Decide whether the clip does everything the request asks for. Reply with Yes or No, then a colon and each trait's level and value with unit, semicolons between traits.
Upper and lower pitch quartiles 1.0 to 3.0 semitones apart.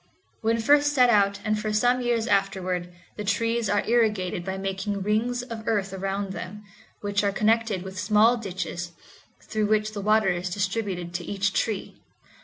Yes: narrow, 2.6 semitones